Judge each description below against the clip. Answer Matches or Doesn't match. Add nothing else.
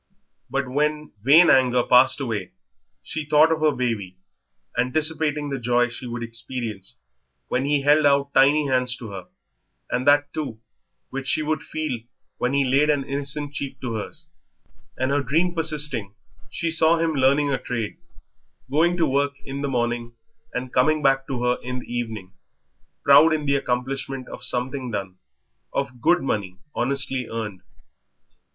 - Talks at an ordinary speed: Matches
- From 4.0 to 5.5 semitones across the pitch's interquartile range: Doesn't match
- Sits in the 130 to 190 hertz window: Matches